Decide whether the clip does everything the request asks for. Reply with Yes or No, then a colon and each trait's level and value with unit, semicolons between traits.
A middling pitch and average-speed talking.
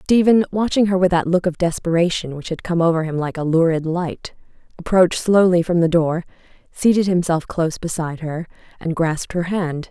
Yes: medium, 170 Hz; average, 190 wpm